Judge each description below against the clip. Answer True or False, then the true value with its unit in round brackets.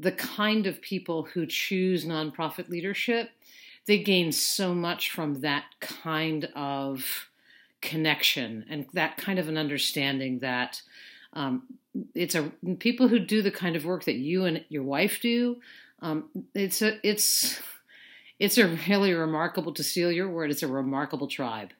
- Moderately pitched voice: True (175 Hz)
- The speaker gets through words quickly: False (155 wpm)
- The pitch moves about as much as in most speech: True (5.0 semitones)